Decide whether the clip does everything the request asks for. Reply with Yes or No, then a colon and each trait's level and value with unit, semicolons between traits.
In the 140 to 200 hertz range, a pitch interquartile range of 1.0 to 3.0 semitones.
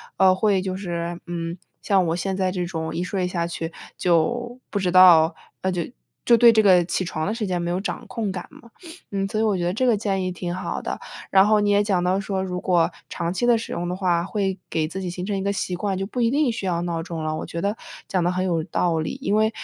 Yes: medium, 185 Hz; average, 2.7 semitones